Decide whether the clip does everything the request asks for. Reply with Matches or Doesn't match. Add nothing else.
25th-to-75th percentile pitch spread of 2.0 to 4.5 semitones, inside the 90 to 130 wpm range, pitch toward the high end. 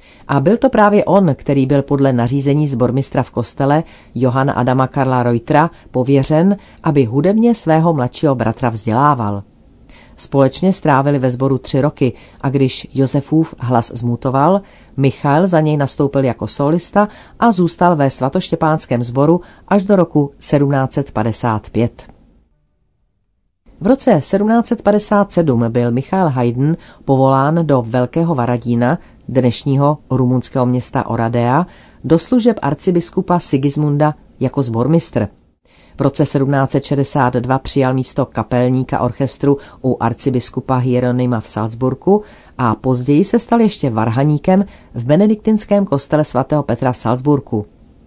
Doesn't match